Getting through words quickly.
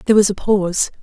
Yes: fast, 235 wpm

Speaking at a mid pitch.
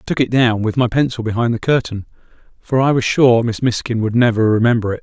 No: low, 120 Hz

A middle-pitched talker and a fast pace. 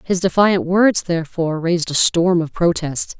No: medium, 175 Hz; average, 170 wpm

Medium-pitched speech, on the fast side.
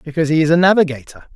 Yes: medium, 155 Hz; fast, 220 wpm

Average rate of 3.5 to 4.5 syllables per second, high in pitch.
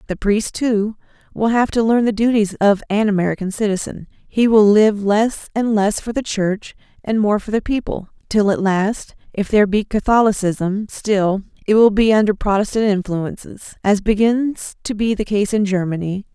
No: 4.8 syllables/s; high, 210 Hz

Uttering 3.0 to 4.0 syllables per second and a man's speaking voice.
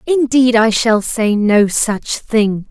No: 3.1 syllables/s; female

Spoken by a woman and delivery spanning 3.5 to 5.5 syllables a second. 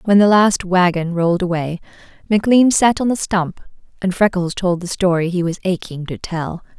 Yes: female; 5.1 syllables/s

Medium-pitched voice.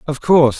Yes: medium, 145 Hz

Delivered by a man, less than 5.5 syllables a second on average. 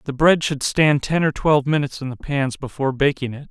No: male; 6.0 syllables/s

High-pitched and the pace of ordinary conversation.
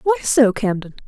Yes: high, 235 Hz; average, 165 wpm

